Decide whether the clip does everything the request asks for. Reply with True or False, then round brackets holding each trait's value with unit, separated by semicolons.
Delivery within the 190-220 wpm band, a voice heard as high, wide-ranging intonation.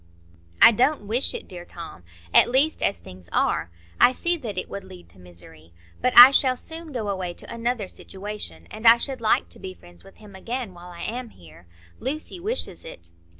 True (200 wpm; 205 Hz; 7.4 semitones)